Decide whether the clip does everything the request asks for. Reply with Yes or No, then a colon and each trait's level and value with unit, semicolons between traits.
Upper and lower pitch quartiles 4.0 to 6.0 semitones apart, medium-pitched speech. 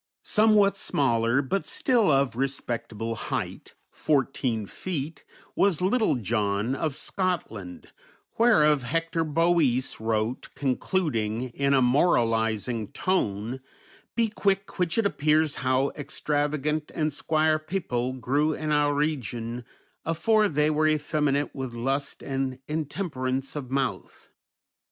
Yes: average, 4.4 semitones; medium, 145 Hz